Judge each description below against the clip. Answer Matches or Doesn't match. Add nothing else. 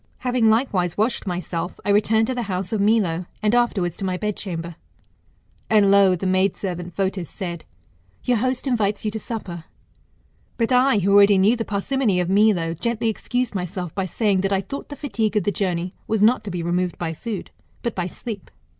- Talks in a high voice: Matches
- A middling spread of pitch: Matches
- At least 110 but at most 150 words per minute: Doesn't match